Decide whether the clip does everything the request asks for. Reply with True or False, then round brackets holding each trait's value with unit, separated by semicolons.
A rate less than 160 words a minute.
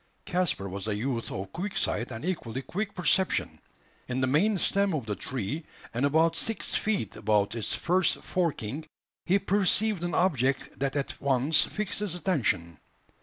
False (165 wpm)